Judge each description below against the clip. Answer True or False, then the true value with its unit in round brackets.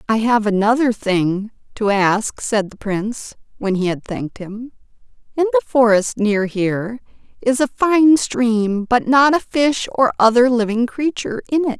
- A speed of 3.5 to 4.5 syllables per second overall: True (4.4 syllables/s)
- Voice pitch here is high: True (230 Hz)